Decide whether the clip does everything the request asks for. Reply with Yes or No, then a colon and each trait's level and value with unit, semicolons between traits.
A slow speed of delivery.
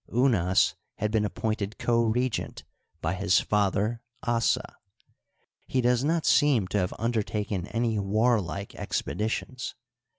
Yes: slow, 120 wpm